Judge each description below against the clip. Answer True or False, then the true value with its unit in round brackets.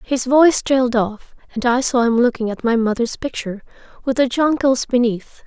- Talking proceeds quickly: False (185 wpm)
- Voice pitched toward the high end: True (245 Hz)